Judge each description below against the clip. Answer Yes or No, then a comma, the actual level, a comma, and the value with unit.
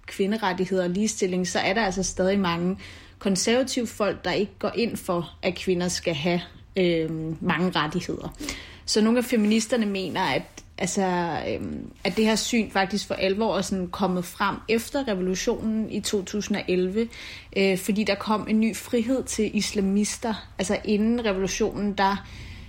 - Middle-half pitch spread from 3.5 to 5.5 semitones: No, average, 2.8 semitones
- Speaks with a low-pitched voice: No, high, 200 Hz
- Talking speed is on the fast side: No, average, 155 wpm